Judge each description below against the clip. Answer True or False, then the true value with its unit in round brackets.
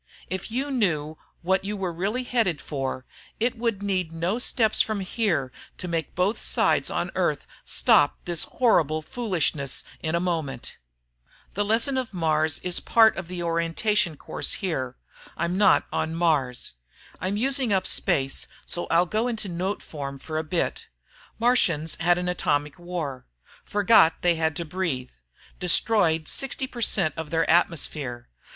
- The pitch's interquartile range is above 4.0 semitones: True (4.9 semitones)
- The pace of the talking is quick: False (155 wpm)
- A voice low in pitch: False (175 Hz)